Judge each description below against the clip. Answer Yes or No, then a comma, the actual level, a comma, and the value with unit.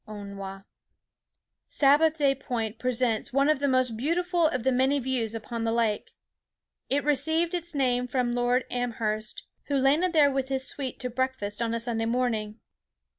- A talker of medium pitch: No, very high, 255 Hz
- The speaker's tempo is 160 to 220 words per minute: Yes, average, 165 wpm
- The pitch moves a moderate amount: Yes, average, 3.6 semitones